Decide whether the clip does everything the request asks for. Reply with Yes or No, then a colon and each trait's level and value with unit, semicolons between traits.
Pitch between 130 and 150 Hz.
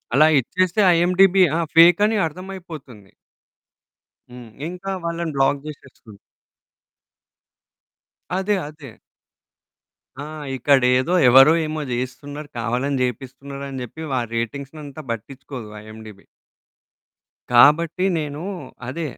Yes: medium, 140 Hz